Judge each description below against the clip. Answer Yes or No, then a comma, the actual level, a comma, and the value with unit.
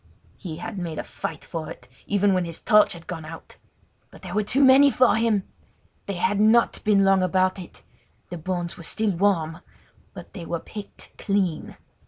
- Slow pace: No, average, 190 wpm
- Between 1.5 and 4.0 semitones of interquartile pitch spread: Yes, average, 3.7 semitones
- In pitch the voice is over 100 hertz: Yes, high, 190 Hz